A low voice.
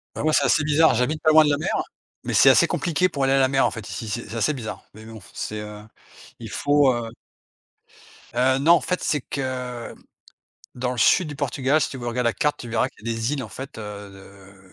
Yes: low, 130 Hz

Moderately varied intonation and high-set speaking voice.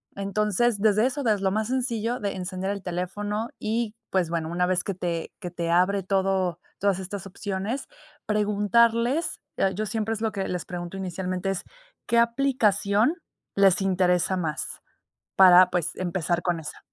Yes: average, 3.1 semitones; high, 195 Hz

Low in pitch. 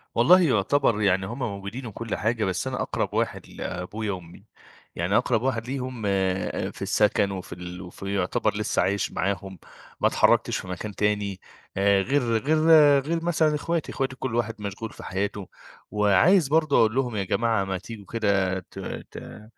Yes: low, 105 Hz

